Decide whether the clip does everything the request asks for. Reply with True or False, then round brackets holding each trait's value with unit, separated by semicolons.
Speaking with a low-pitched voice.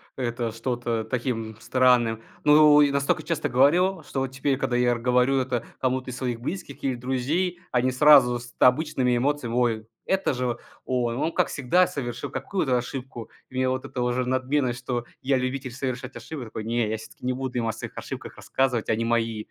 True (125 Hz)